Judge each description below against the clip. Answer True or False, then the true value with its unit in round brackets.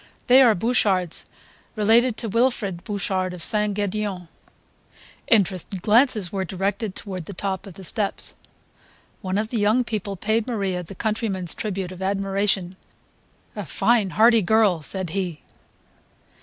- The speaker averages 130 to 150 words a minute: True (140 wpm)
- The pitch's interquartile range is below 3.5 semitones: True (2.8 semitones)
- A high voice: True (200 Hz)